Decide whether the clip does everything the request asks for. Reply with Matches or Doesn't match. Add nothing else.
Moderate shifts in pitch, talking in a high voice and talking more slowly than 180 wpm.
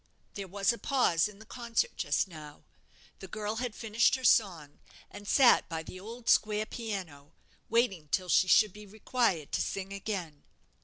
Matches